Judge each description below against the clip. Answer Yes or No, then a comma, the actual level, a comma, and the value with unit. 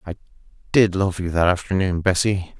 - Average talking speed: Yes, average, 160 wpm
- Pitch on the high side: No, very low, 95 Hz